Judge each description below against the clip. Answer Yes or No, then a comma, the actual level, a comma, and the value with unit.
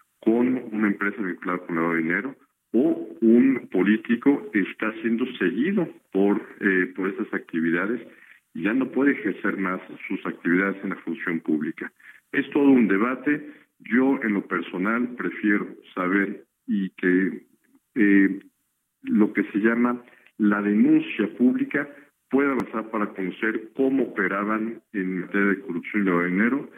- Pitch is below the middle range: Yes, low, 105 Hz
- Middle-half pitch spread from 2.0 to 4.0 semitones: No, average, 4.4 semitones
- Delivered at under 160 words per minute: Yes, average, 140 wpm